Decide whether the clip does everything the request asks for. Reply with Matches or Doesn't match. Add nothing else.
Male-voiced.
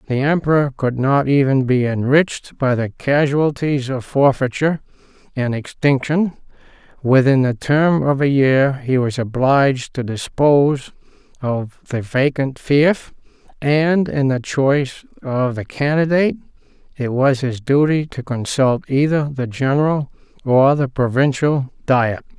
Matches